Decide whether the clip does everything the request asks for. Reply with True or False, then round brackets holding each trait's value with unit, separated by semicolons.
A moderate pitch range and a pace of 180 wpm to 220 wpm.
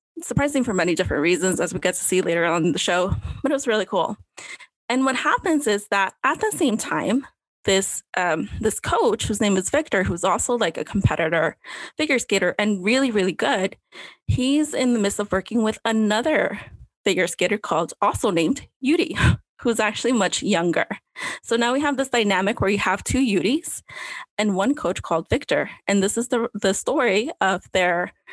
False (5.8 semitones; 190 wpm)